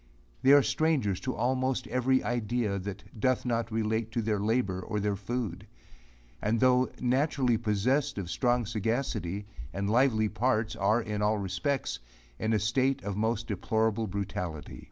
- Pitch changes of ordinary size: Yes, average, 3.5 semitones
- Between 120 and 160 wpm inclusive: Yes, average, 155 wpm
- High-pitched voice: No, low, 110 Hz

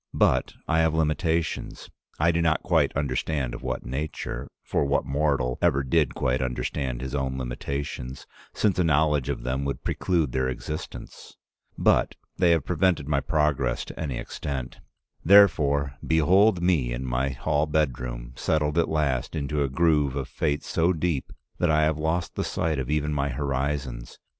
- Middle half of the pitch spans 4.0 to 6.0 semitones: No, average, 3.4 semitones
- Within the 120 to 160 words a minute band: No, average, 170 wpm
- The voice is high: No, very low, 75 Hz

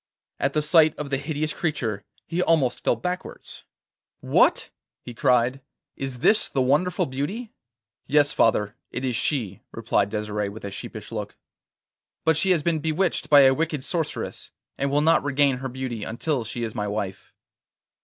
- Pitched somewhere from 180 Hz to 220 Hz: No, low, 135 Hz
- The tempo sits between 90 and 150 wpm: No, average, 165 wpm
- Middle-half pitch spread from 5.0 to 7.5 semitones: Yes, average, 5.3 semitones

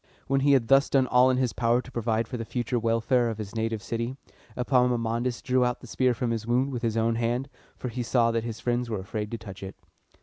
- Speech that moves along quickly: Yes, fast, 245 wpm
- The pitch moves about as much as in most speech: No, narrow, 1.8 semitones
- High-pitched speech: No, low, 120 Hz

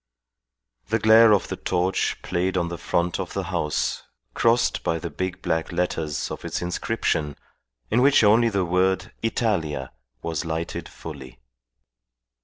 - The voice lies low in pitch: Yes, very low, 90 Hz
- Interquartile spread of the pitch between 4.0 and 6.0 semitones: Yes, average, 4.6 semitones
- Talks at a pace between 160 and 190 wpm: No, average, 145 wpm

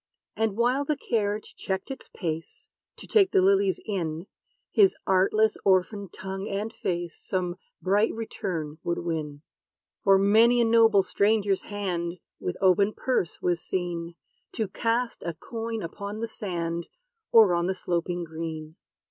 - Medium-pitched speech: No, high, 195 Hz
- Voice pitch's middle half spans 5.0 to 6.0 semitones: No, average, 4.5 semitones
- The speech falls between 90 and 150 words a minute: Yes, average, 145 wpm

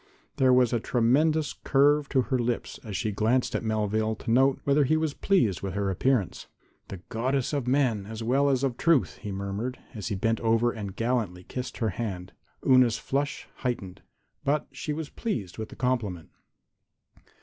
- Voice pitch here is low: Yes, low, 120 Hz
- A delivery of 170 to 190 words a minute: Yes, average, 180 wpm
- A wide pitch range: No, average, 4.2 semitones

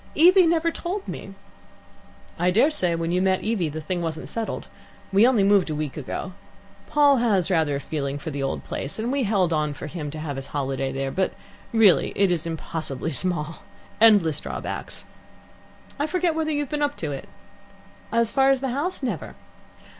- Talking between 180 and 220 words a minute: Yes, average, 190 wpm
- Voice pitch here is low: No, medium, 185 Hz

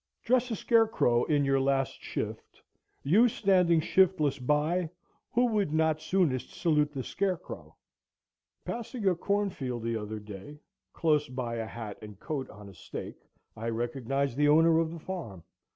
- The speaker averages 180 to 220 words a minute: No, average, 150 wpm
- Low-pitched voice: No, medium, 150 Hz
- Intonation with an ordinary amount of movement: No, wide, 6.9 semitones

